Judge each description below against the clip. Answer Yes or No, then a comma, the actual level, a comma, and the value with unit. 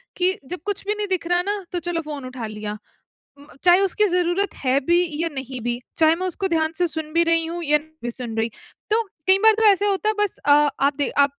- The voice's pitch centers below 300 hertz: No, very high, 335 Hz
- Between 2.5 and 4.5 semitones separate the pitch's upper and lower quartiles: No, average, 5.0 semitones